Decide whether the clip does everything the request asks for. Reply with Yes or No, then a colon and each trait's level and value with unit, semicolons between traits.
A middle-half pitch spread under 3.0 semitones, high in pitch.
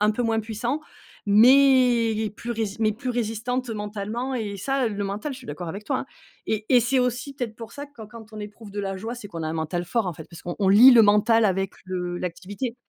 No: average, 3.3 semitones; high, 220 Hz